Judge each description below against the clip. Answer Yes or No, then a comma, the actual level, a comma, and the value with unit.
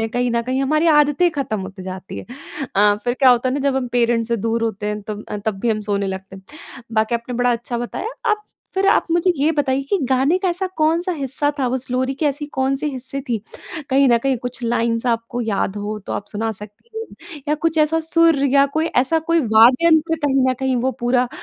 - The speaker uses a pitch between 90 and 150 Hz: No, very high, 255 Hz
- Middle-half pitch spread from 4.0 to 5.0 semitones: Yes, average, 4.6 semitones